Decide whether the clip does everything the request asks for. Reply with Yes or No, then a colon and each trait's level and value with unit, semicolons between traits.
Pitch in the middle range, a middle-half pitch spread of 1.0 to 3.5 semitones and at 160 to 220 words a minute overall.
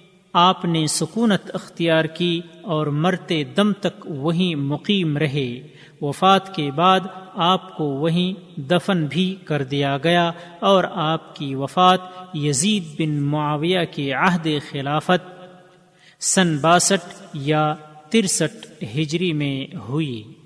No: medium, 170 Hz; average, 3.2 semitones; average, 115 wpm